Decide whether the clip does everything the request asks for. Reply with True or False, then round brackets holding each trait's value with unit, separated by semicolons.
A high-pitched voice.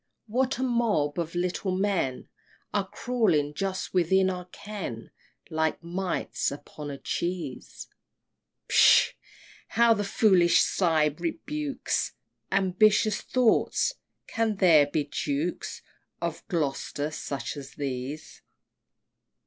False (180 Hz)